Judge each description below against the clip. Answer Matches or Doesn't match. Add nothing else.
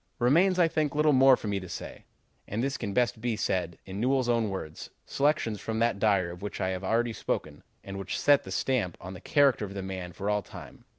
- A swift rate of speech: Matches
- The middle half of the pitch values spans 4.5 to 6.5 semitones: Matches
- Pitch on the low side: Matches